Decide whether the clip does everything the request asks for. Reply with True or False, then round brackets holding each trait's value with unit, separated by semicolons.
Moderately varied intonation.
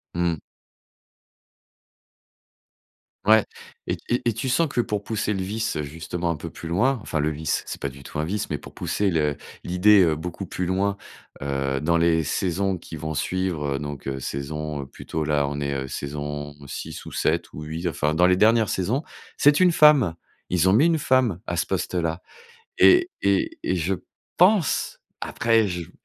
False (5.8 semitones)